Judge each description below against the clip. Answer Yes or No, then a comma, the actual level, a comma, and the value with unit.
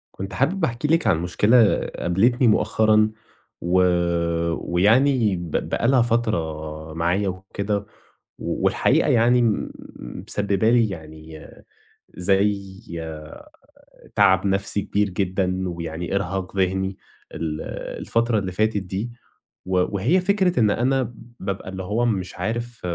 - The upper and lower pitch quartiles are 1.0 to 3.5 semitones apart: No, average, 4.0 semitones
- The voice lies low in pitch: Yes, low, 100 Hz